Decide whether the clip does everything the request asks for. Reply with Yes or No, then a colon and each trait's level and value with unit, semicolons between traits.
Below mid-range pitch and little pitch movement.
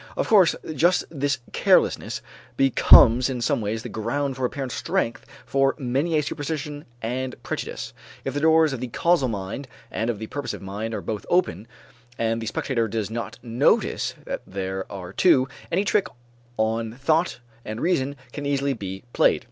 No: low, 130 Hz; average, 4.4 semitones